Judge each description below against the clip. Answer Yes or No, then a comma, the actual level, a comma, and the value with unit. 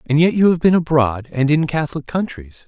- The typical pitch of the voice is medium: Yes, medium, 150 Hz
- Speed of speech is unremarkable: No, fast, 225 wpm